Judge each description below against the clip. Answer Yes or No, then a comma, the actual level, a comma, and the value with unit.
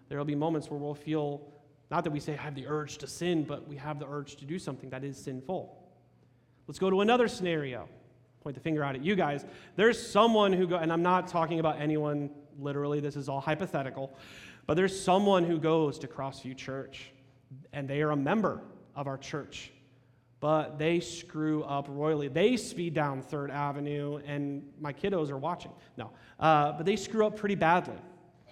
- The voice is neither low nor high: Yes, medium, 150 Hz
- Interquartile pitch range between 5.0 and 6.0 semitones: No, average, 3.4 semitones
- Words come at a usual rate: Yes, average, 195 wpm